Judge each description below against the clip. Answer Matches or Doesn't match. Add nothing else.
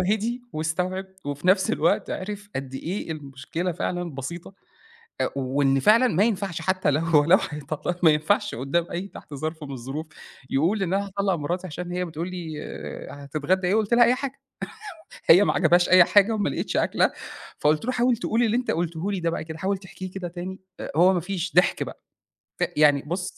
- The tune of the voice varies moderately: Matches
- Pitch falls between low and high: Matches